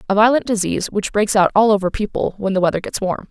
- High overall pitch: Yes, high, 205 Hz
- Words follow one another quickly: Yes, fast, 255 wpm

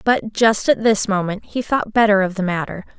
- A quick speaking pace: Yes, fast, 220 wpm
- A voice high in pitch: Yes, high, 210 Hz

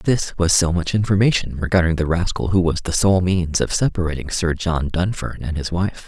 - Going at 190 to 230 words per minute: Yes, fast, 205 wpm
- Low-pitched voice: Yes, very low, 90 Hz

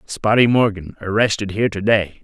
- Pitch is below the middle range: Yes, low, 105 Hz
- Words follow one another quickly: No, average, 160 wpm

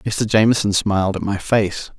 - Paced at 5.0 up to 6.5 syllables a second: No, 4.8 syllables/s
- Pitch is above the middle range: No, low, 105 Hz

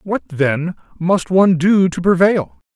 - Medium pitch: Yes, medium, 170 Hz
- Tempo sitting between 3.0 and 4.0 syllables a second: Yes, 3.9 syllables/s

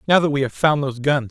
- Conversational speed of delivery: No, fast, 320 wpm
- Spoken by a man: Yes, male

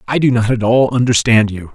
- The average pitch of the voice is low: Yes, low, 115 Hz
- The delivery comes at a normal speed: No, fast, 240 wpm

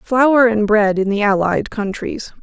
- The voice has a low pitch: No, high, 215 Hz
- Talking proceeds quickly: No, average, 175 wpm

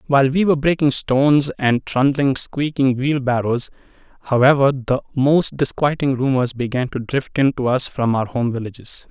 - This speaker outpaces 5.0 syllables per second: No, 4.9 syllables/s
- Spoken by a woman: No, male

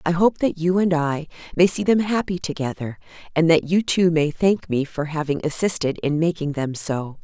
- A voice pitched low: No, medium, 165 Hz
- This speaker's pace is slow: No, fast, 205 wpm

